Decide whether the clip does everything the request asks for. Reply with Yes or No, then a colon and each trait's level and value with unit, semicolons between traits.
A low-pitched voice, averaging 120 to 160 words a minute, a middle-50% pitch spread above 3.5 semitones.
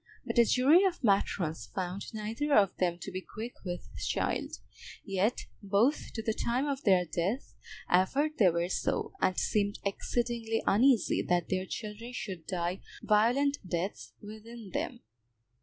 No: high, 210 Hz; average, 150 wpm; average, 4.3 semitones